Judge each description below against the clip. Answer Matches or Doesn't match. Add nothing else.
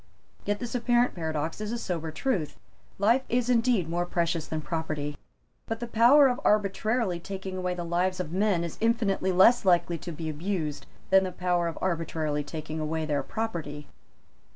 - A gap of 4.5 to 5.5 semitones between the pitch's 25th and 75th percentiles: Matches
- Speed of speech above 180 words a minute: Doesn't match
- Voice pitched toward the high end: Doesn't match